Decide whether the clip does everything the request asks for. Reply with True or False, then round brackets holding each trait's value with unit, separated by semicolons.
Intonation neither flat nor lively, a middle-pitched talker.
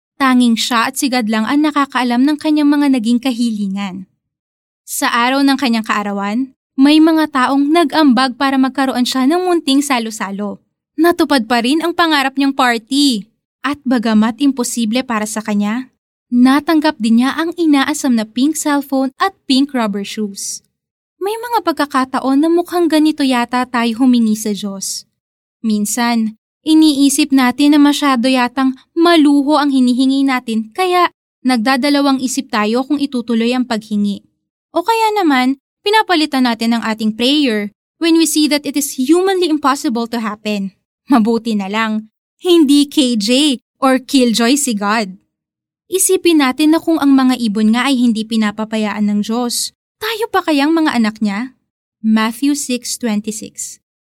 False (4.2 semitones; 260 Hz)